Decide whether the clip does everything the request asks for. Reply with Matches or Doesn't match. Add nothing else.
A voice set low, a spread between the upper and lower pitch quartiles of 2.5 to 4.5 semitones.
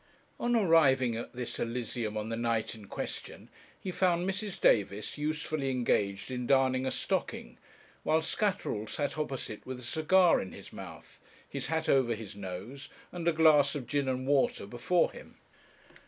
Doesn't match